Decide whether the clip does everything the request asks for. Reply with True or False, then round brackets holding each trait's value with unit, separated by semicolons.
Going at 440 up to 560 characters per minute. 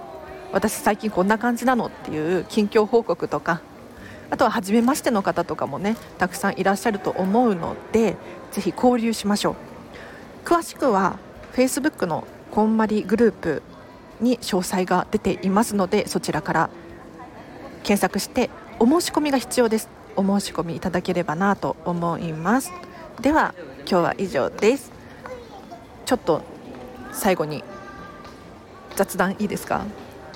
False (295 characters per minute)